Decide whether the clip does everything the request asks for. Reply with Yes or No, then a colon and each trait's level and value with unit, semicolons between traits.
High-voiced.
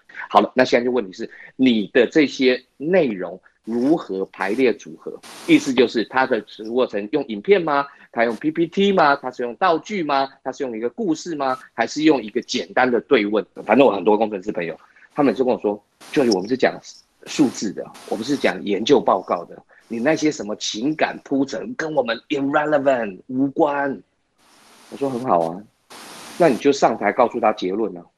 No: low, 135 Hz